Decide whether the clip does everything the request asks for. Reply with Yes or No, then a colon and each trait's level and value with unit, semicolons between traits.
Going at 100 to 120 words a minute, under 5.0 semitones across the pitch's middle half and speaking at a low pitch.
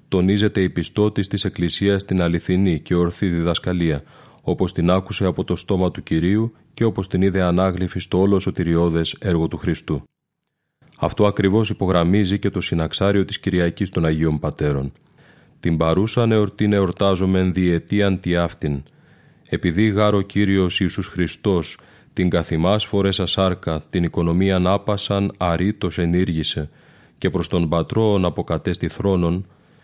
No: average, 135 wpm; narrow, 2.6 semitones; very low, 95 Hz